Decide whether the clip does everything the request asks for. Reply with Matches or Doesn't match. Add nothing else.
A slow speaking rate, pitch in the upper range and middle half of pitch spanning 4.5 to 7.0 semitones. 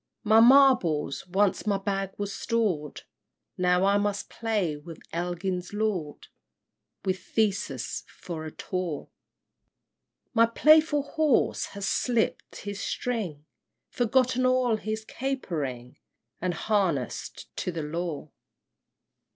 Matches